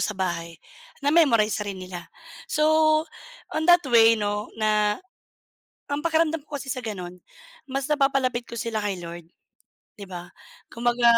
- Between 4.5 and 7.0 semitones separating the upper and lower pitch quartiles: Yes, wide, 5.6 semitones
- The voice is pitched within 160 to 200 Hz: No, high, 225 Hz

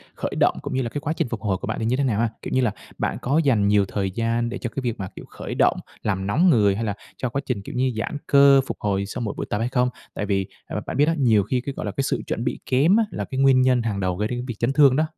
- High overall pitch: No, low, 120 Hz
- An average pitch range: Yes, average, 4.5 semitones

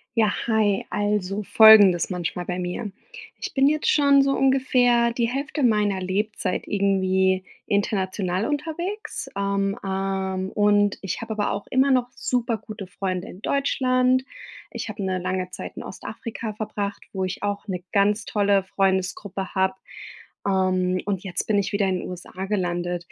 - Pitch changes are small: No, average, 3.1 semitones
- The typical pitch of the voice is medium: No, high, 200 Hz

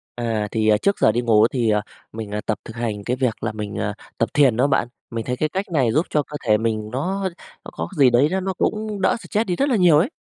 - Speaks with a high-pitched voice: No, low, 120 Hz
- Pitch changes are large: Yes, wide, 7.8 semitones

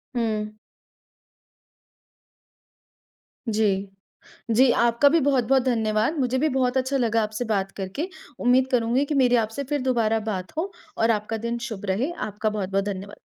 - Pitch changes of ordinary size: Yes, average, 3.5 semitones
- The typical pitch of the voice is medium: No, high, 230 Hz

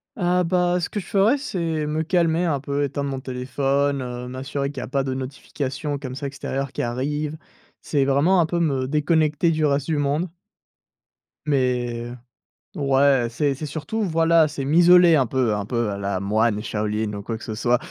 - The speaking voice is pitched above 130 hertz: Yes, medium, 140 Hz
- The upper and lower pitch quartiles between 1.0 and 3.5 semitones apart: No, average, 3.9 semitones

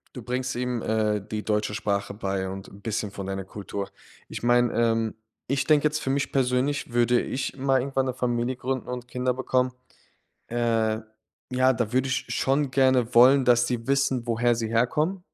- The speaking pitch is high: No, low, 120 Hz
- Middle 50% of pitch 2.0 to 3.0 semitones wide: Yes, narrow, 2.6 semitones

